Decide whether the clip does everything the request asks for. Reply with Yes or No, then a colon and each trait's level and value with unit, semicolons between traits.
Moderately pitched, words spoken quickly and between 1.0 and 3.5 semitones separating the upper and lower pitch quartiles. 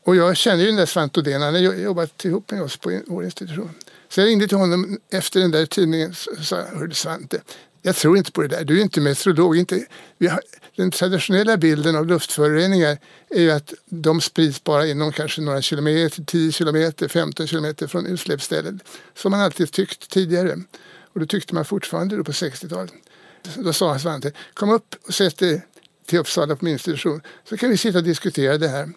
Yes: medium, 170 Hz; fast, 200 wpm; average, 3.0 semitones